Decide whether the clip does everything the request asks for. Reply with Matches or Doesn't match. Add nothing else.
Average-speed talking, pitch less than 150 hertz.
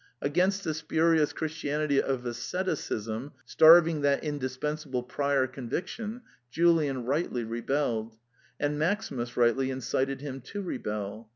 Doesn't match